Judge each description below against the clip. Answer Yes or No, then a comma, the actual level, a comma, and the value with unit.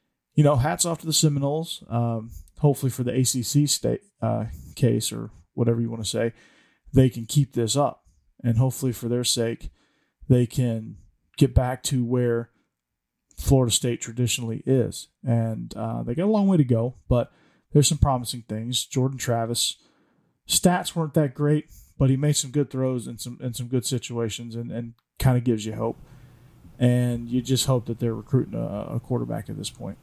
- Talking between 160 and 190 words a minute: Yes, average, 185 wpm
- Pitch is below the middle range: Yes, low, 125 Hz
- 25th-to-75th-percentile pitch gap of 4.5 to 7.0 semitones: No, narrow, 2.6 semitones